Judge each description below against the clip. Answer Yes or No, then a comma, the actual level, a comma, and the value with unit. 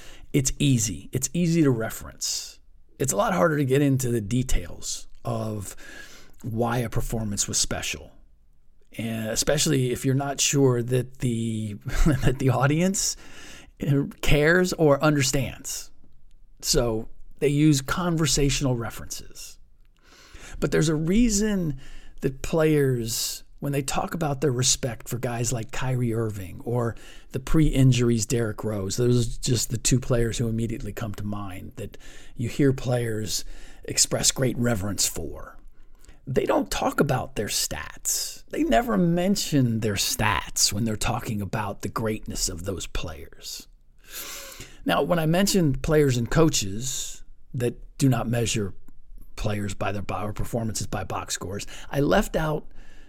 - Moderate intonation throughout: Yes, average, 4.6 semitones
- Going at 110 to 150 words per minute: Yes, average, 140 wpm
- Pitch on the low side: Yes, low, 120 Hz